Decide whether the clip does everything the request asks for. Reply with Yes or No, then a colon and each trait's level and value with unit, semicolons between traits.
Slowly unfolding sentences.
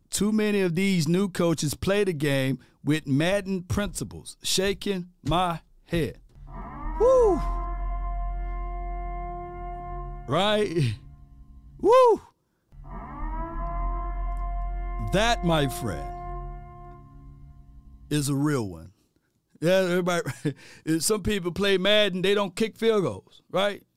Yes: slow, 95 wpm